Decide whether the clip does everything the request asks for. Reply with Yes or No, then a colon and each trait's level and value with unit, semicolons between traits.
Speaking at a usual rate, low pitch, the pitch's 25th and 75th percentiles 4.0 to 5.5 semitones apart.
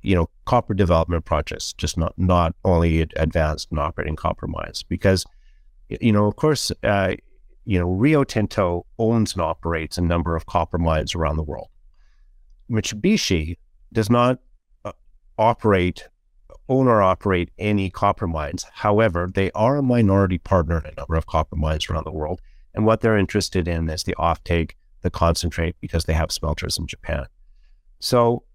Yes: average, 165 wpm; very low, 90 Hz; average, 4.3 semitones